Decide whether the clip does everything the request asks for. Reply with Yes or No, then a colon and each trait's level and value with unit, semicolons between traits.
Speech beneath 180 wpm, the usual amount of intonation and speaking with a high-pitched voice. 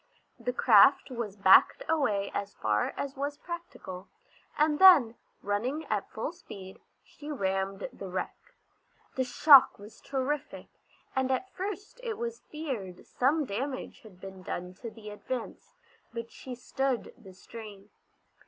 No: average, 140 wpm; wide, 6.7 semitones; very high, 250 Hz